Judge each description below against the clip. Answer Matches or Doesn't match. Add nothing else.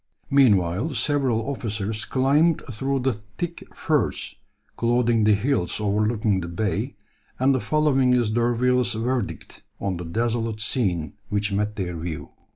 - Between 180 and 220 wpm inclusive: Doesn't match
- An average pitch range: Matches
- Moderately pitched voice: Doesn't match